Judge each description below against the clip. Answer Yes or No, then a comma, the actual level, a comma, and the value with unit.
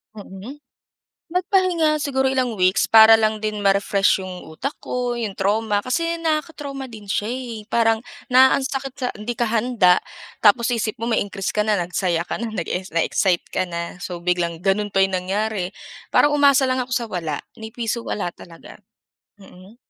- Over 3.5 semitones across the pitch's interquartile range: Yes, average, 4.8 semitones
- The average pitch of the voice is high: Yes, high, 220 Hz